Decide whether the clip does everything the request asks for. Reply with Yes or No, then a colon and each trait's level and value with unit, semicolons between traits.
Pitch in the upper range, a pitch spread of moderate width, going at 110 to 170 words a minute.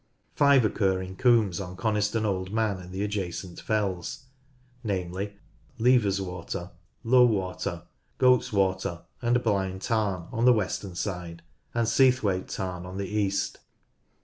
No: low, 100 Hz; average, 3.4 semitones; average, 150 wpm